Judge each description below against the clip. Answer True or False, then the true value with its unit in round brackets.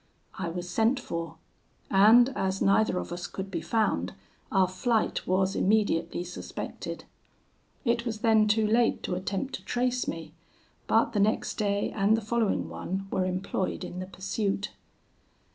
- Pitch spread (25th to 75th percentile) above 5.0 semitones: False (3.2 semitones)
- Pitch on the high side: True (200 Hz)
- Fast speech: False (155 wpm)